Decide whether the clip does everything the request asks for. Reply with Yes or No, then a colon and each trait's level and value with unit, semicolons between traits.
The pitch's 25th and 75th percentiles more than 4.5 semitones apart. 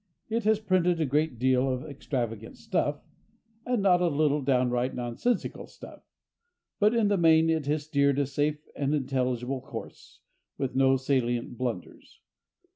No: average, 4.2 semitones